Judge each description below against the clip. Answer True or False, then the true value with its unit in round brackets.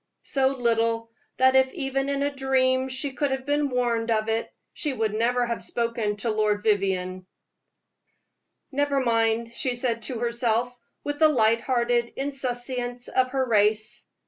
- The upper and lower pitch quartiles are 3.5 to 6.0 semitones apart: False (2.7 semitones)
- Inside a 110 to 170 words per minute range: True (155 wpm)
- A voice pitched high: True (245 Hz)